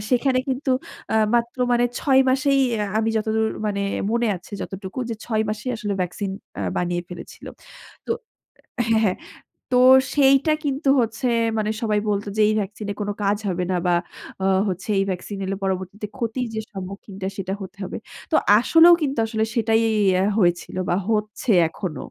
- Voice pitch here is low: No, high, 215 Hz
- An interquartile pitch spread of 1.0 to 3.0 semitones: No, average, 3.8 semitones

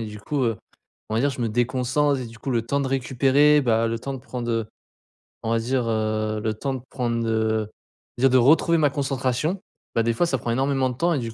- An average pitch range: Yes, average, 3.2 semitones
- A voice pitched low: Yes, low, 125 Hz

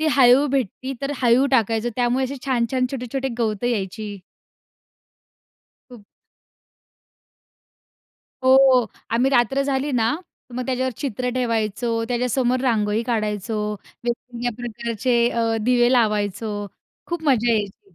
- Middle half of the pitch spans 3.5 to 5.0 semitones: No, narrow, 2.6 semitones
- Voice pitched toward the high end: Yes, high, 240 Hz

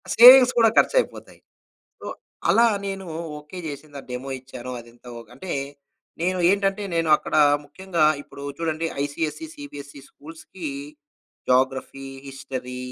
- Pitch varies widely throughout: Yes, wide, 6.0 semitones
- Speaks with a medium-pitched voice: Yes, medium, 155 Hz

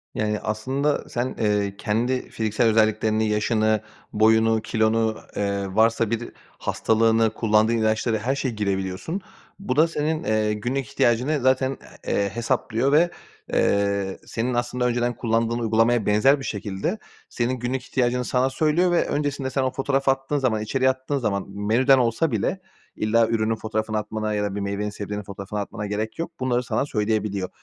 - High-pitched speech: No, low, 115 Hz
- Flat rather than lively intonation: No, average, 3.4 semitones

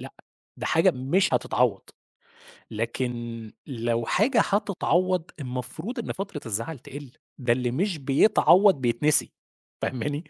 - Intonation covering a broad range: Yes, wide, 7.3 semitones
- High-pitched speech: No, medium, 140 Hz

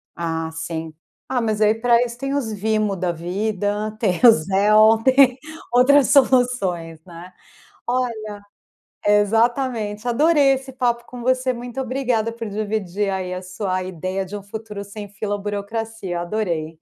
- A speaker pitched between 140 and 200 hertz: No, high, 215 Hz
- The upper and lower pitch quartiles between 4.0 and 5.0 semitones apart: Yes, average, 4.3 semitones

